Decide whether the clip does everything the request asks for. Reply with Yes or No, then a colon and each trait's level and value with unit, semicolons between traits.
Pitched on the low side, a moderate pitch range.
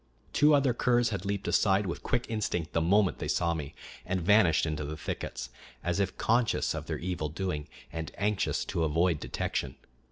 Yes: very low, 90 Hz; average, 4.5 semitones